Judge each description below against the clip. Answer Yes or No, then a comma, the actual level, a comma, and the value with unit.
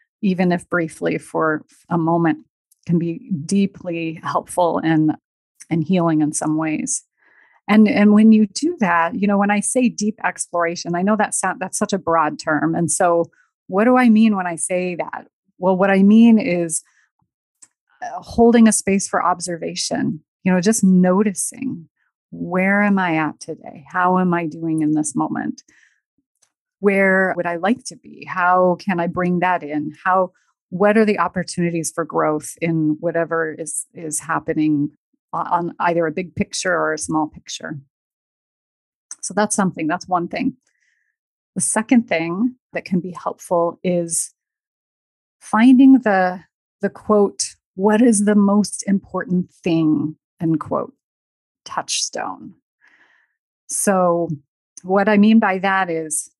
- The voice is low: No, medium, 180 Hz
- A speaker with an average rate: Yes, average, 150 wpm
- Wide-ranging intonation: No, average, 4.0 semitones